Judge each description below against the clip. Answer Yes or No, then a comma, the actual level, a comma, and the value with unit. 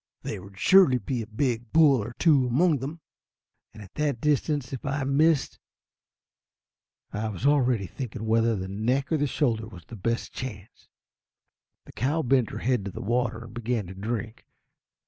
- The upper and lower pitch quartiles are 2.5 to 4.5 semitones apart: Yes, average, 4.1 semitones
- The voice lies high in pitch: No, low, 120 Hz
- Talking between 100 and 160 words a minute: No, average, 175 wpm